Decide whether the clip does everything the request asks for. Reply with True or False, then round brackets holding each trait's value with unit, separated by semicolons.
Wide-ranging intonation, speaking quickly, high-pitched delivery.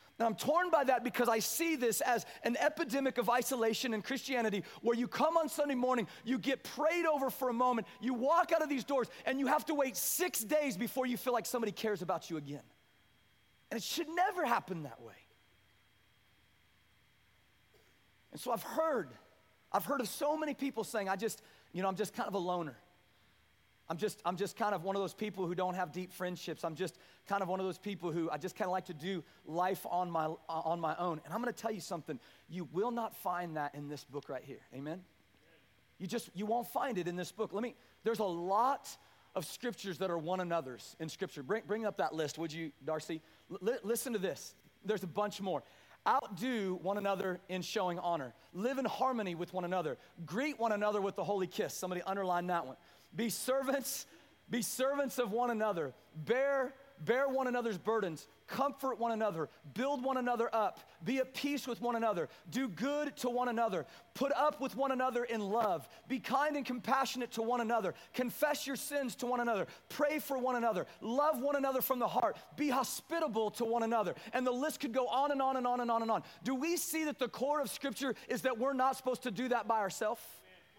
True (6.3 semitones; 215 wpm; 225 Hz)